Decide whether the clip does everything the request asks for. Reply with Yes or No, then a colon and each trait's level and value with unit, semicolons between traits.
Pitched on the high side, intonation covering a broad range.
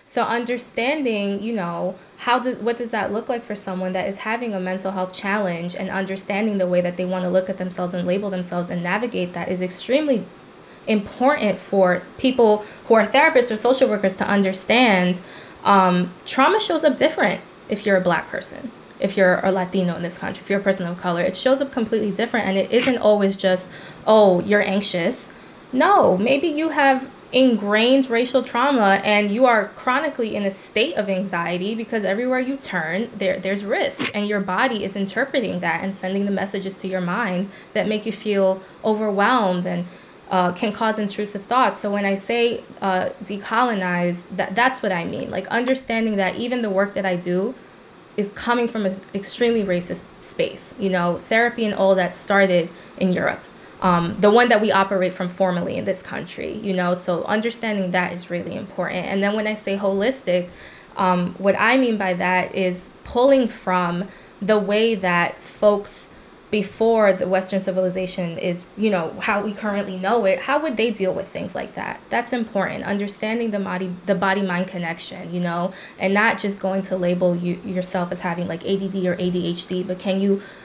No: high, 195 Hz; average, 3.3 semitones